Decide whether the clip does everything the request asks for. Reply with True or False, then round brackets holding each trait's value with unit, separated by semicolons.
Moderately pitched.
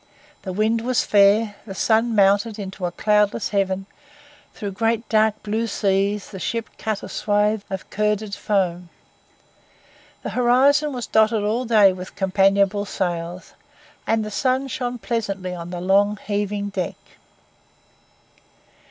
False (205 Hz)